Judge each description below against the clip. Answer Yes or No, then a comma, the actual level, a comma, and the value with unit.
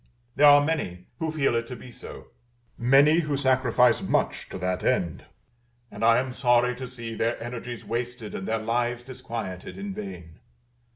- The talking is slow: No, average, 170 wpm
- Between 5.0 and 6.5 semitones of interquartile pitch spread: No, average, 3.1 semitones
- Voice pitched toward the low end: Yes, low, 120 Hz